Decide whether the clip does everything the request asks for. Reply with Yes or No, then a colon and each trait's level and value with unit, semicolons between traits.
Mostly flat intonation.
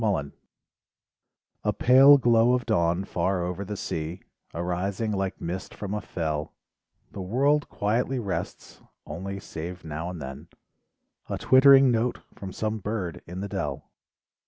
No: average, 4.7 semitones